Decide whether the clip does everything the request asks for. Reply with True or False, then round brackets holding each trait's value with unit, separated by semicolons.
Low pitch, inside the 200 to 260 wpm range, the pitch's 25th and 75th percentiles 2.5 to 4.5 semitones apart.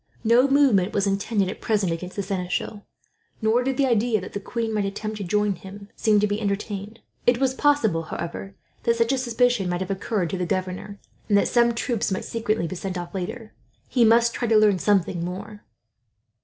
False (210 Hz; 205 wpm; 3.3 semitones)